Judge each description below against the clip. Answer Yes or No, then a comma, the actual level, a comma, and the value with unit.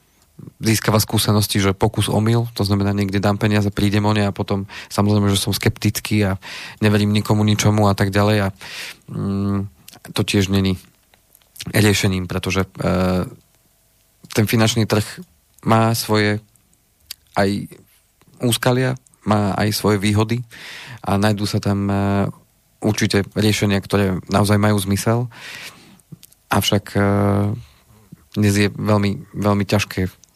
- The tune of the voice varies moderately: No, narrow, 1.4 semitones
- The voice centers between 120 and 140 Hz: No, low, 105 Hz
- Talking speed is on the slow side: No, average, 125 wpm